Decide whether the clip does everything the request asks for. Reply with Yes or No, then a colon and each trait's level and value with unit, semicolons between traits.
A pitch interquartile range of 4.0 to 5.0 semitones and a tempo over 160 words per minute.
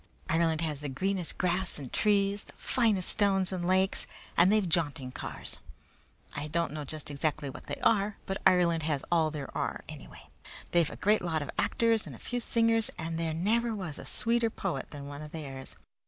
Yes: average, 4.7 semitones; average, 195 wpm